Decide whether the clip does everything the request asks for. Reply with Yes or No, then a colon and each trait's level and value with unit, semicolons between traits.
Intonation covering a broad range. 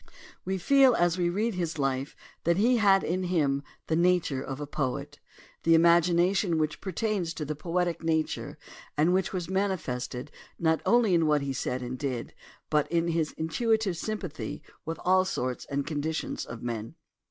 No: average, 4.1 semitones